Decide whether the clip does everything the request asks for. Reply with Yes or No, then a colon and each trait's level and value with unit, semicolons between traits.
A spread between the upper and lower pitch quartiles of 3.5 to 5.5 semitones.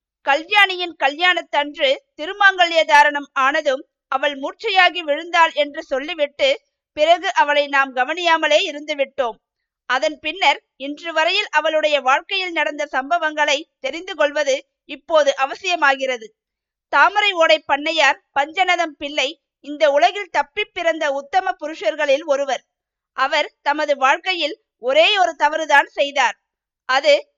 No: average, 3.0 semitones